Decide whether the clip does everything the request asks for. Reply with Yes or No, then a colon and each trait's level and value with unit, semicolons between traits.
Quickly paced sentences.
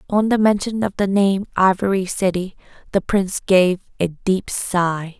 No: average, 160 wpm